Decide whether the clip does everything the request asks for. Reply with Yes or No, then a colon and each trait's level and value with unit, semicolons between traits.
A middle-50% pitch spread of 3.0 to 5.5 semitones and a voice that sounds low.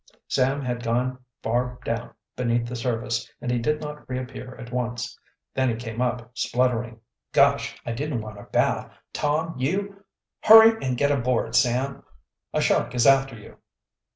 No: narrow, 2.5 semitones; low, 125 Hz